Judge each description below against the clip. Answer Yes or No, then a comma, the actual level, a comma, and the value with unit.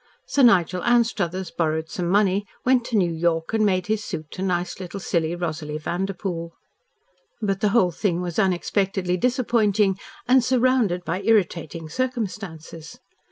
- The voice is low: No, medium, 185 Hz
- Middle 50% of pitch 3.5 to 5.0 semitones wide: Yes, average, 4.1 semitones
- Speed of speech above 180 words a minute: No, average, 145 wpm